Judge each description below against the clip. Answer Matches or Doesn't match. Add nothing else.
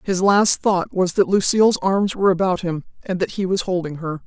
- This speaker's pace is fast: Matches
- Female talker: Matches